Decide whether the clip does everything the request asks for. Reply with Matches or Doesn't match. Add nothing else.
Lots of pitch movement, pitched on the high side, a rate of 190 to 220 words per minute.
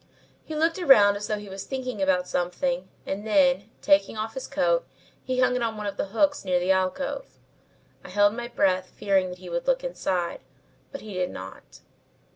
Matches